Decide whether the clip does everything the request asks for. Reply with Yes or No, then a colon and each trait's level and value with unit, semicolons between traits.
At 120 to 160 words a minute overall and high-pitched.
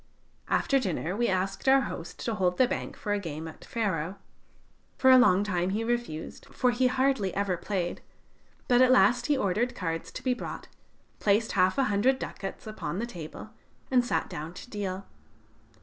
No: average, 180 wpm; high, 205 Hz